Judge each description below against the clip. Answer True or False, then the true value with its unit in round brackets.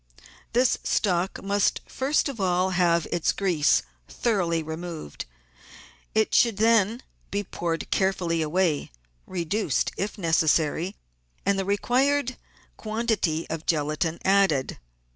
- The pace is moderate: False (115 wpm)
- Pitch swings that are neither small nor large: True (4.4 semitones)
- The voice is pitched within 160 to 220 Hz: True (185 Hz)